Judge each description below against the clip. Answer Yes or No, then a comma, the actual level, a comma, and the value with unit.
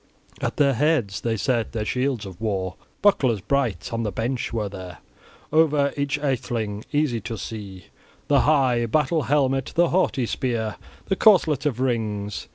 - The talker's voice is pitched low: Yes, low, 120 Hz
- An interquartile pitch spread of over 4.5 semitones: Yes, average, 5.0 semitones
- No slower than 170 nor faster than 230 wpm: No, average, 160 wpm